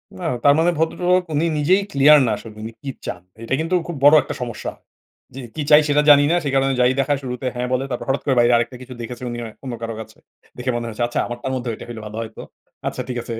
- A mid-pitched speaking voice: No, low, 130 Hz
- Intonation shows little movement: No, average, 3.5 semitones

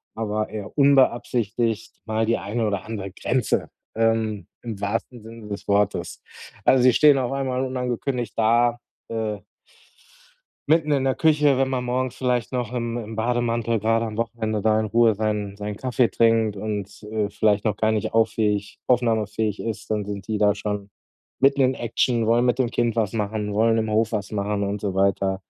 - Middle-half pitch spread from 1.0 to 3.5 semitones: Yes, narrow, 2.5 semitones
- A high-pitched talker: No, low, 110 Hz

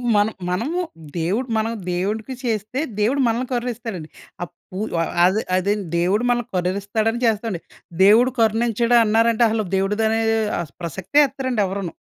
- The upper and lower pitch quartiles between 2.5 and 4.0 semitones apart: Yes, average, 3.5 semitones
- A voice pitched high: Yes, high, 220 Hz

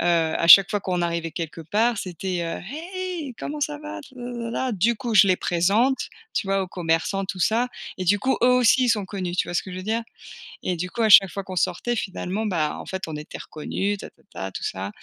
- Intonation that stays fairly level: No, average, 5.3 semitones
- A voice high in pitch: Yes, high, 195 Hz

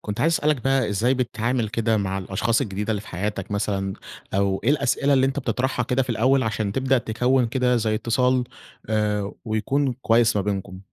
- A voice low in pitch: Yes, low, 115 Hz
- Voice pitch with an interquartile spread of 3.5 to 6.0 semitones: Yes, average, 3.8 semitones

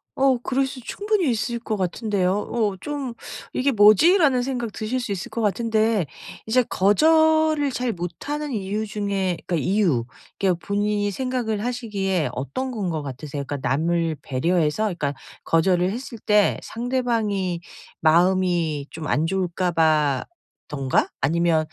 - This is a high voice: Yes, high, 205 Hz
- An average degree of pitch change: No, wide, 6.3 semitones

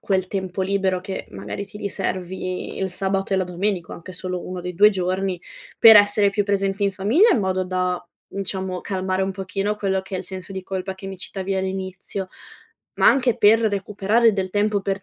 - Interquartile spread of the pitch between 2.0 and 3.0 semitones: No, narrow, 1.4 semitones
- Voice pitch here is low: No, high, 190 Hz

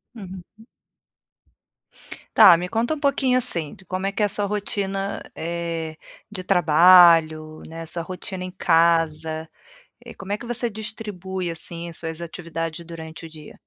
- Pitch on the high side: No, medium, 175 Hz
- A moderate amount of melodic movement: Yes, average, 3.3 semitones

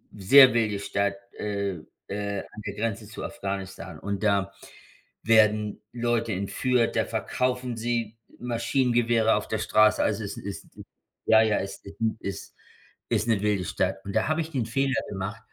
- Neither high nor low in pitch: No, low, 110 Hz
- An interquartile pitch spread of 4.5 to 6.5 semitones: No, average, 2.8 semitones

